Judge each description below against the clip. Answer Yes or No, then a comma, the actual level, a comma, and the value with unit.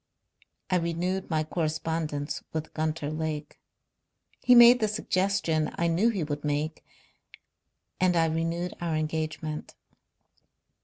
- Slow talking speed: Yes, slow, 115 wpm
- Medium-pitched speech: Yes, medium, 160 Hz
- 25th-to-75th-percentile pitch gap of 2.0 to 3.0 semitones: Yes, narrow, 2.6 semitones